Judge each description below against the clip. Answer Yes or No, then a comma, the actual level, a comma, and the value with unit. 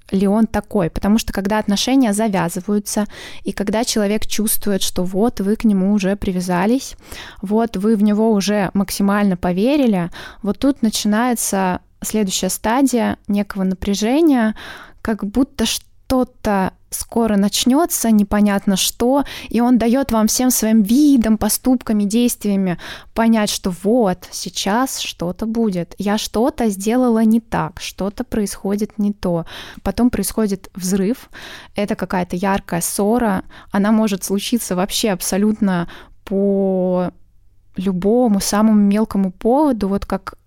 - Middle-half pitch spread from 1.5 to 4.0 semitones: Yes, narrow, 2.5 semitones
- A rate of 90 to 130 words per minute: Yes, average, 125 wpm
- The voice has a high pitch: Yes, high, 210 Hz